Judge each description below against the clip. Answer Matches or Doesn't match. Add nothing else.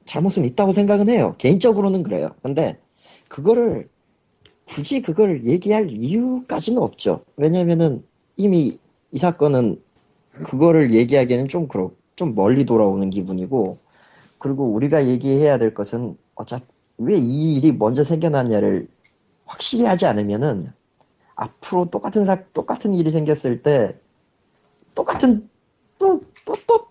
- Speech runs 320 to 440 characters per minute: Doesn't match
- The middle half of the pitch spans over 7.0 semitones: Matches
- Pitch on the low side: Doesn't match